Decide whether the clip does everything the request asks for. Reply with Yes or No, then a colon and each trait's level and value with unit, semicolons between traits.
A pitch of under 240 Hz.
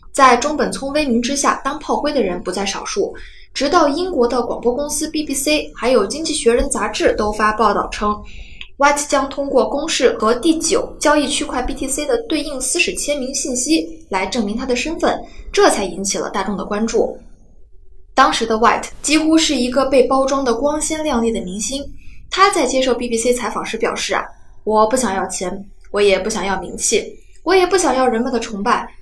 No: very high, 270 Hz